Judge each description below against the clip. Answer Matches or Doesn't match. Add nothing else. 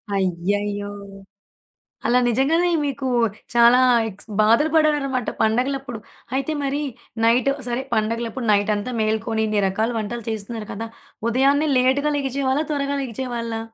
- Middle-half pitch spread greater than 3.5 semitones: Matches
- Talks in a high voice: Matches